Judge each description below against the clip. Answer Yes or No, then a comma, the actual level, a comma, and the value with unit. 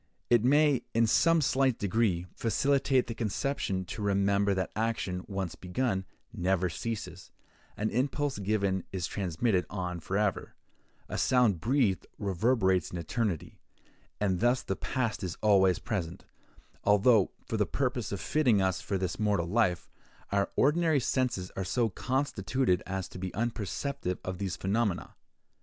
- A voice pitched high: No, low, 105 Hz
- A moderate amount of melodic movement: Yes, average, 4.5 semitones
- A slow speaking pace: No, average, 145 wpm